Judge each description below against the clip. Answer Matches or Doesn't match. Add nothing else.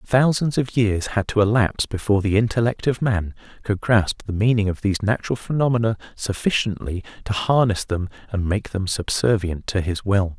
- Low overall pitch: Matches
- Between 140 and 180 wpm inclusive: Matches